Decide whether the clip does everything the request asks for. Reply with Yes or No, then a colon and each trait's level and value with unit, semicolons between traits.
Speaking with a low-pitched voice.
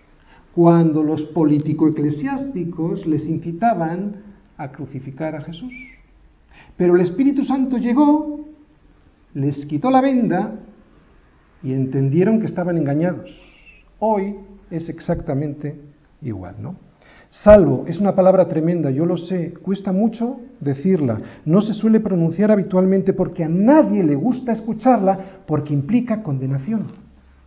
No: medium, 180 Hz